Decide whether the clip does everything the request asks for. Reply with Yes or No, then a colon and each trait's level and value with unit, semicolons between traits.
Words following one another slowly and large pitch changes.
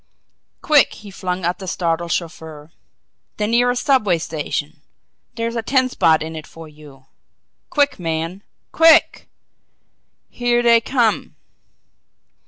Yes: slow, 120 wpm; wide, 6.9 semitones